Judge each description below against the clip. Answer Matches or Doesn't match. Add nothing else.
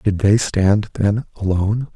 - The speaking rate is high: Doesn't match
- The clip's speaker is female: Doesn't match